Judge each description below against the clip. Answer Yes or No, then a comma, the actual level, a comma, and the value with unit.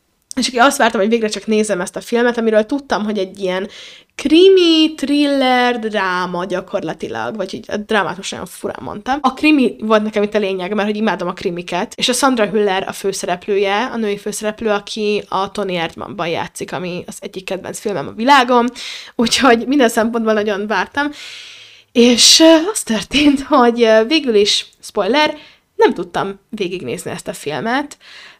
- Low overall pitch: No, high, 220 Hz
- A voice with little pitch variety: No, average, 3.9 semitones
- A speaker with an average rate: No, fast, 160 wpm